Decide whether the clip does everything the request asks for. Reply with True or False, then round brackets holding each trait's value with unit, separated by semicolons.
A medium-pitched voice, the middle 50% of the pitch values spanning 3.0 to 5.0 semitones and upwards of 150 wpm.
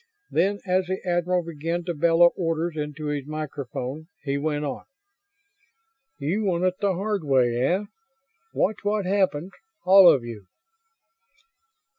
False (170 Hz; 4.0 semitones; 135 wpm)